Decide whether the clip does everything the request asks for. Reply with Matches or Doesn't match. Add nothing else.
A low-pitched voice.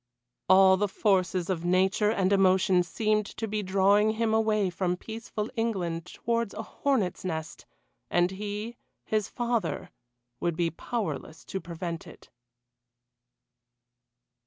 Doesn't match